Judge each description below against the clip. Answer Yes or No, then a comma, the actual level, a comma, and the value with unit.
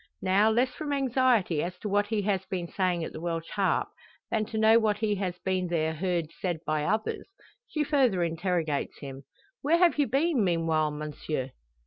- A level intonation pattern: No, average, 5.0 semitones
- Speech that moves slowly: No, average, 180 wpm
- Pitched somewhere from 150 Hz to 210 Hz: Yes, high, 190 Hz